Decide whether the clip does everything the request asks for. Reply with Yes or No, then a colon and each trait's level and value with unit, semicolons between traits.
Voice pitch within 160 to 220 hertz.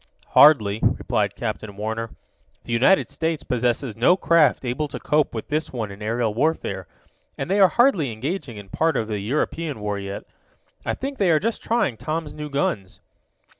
No: low, 130 Hz